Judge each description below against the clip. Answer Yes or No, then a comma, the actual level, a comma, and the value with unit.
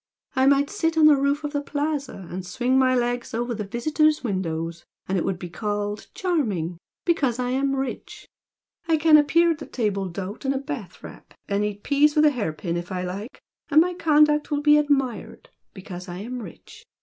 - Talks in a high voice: Yes, very high, 255 Hz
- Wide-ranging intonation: Yes, wide, 7.0 semitones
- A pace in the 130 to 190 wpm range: No, fast, 205 wpm